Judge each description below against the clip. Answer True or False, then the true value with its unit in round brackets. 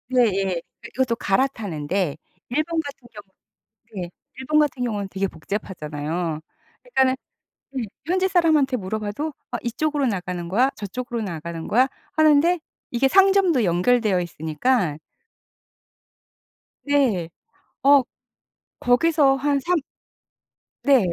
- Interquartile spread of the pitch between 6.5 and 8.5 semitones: True (7.3 semitones)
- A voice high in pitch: True (245 Hz)